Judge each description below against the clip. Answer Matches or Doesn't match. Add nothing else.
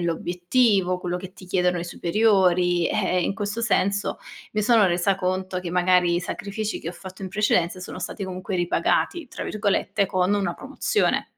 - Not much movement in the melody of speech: Matches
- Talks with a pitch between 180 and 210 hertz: Matches